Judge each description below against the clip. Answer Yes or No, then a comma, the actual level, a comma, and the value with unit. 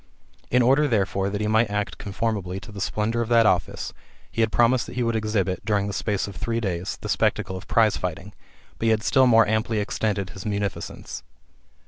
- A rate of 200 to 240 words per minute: Yes, fast, 205 wpm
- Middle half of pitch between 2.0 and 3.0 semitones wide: Yes, narrow, 2.5 semitones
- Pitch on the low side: Yes, low, 105 Hz